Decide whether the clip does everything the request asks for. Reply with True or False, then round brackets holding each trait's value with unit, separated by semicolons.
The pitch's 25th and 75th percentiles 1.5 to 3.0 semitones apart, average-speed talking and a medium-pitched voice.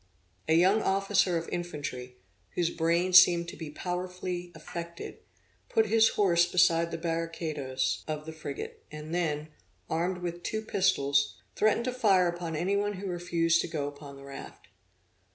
True (2.6 semitones; 155 wpm; 170 Hz)